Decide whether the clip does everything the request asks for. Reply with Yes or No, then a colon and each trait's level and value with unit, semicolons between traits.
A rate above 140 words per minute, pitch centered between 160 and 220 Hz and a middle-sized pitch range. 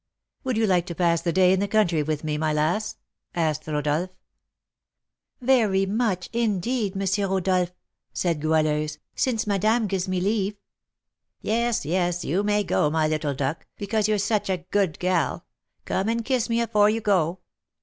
Yes: average, 165 wpm; high, 190 Hz; average, 4.4 semitones